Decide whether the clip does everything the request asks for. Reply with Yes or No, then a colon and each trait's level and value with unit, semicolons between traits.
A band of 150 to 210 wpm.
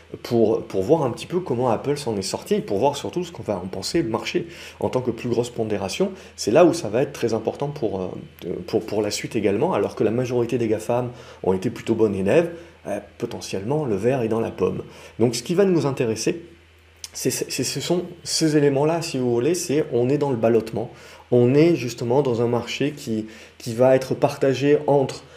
No: fast, 220 wpm